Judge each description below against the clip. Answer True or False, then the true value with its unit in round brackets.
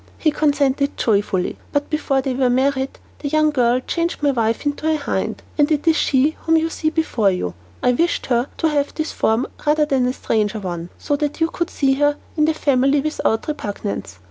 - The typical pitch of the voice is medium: False (280 Hz)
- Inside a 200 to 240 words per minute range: True (205 wpm)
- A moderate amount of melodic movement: True (3.7 semitones)